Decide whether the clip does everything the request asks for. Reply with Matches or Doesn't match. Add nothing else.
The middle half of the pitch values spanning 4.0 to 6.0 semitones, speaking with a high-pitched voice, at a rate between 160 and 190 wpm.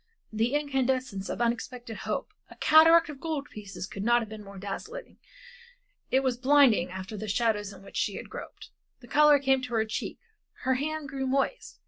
Matches